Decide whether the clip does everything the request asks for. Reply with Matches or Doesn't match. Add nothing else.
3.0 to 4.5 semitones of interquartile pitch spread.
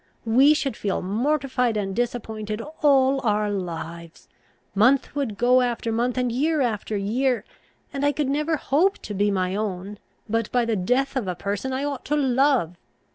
Doesn't match